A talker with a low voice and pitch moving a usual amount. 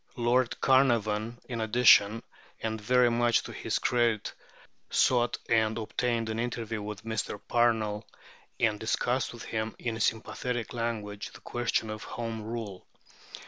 No: low, 115 Hz; narrow, 1.7 semitones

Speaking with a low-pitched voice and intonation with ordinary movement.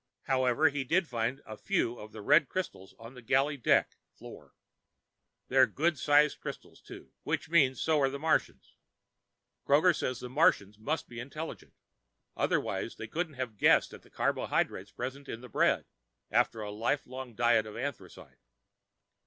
Yes: low, 130 Hz; average, 4.4 semitones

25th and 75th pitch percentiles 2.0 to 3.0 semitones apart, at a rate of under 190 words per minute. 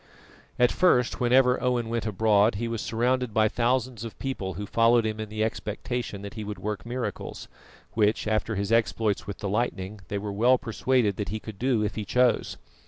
No: average, 2.7 semitones; average, 195 wpm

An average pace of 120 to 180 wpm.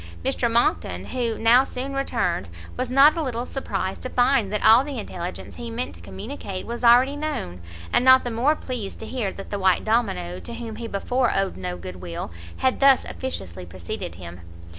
No: average, 195 wpm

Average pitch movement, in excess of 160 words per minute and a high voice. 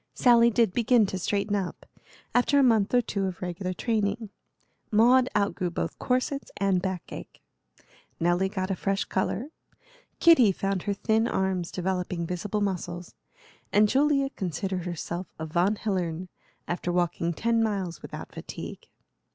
No: average, 3.9 semitones; average, 145 wpm; high, 195 Hz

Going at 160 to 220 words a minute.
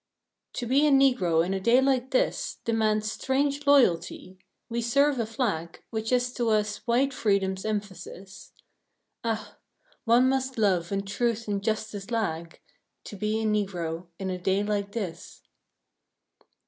No: average, 150 wpm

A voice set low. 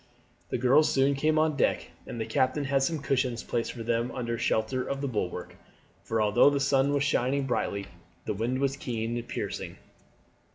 Yes: low, 130 Hz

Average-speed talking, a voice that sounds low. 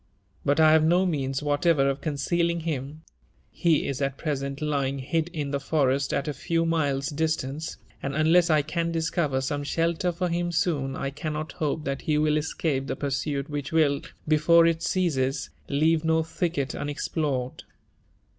No: average, 160 wpm; medium, 150 Hz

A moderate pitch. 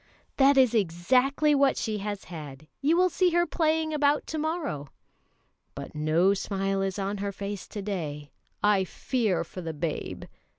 No: high, 205 Hz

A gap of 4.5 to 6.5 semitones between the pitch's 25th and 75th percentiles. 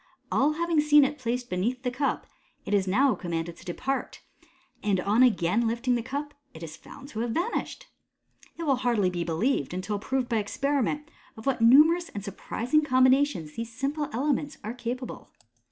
Yes: average, 5.3 semitones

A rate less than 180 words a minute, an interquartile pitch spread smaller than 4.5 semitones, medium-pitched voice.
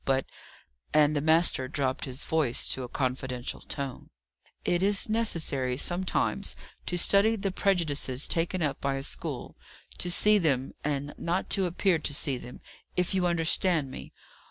No: average, 155 wpm; average, 5.0 semitones; medium, 155 Hz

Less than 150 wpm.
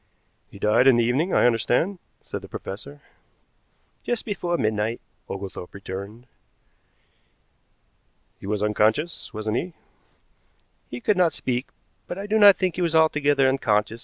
Yes: average, 140 wpm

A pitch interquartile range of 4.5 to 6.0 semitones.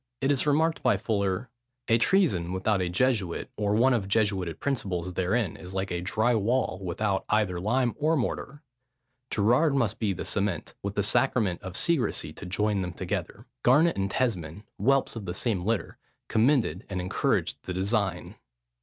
Yes: average, 4.8 semitones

